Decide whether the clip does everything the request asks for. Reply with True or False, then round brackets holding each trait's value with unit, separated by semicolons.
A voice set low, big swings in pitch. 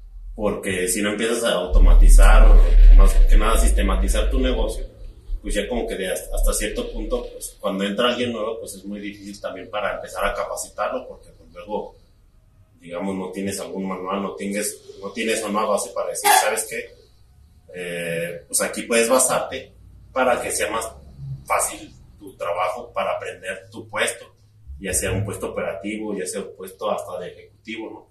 False (100 Hz; 4.6 semitones)